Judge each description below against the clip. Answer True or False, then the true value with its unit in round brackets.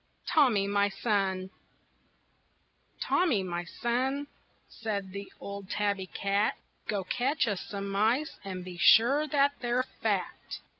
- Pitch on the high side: True (205 Hz)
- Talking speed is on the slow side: True (120 wpm)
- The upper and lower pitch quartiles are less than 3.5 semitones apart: False (4.2 semitones)